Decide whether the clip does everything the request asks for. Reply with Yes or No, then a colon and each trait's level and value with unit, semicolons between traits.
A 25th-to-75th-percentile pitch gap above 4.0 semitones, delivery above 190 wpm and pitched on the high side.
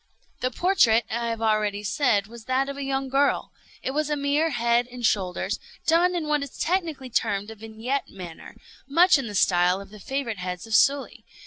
Yes: average, 4.8 semitones; average, 200 wpm; high, 245 Hz